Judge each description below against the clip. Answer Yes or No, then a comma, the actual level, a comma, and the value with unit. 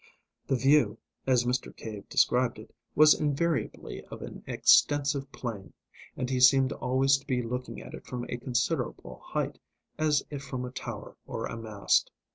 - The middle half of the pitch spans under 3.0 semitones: Yes, narrow, 2.4 semitones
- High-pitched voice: No, low, 130 Hz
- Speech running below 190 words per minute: Yes, average, 165 wpm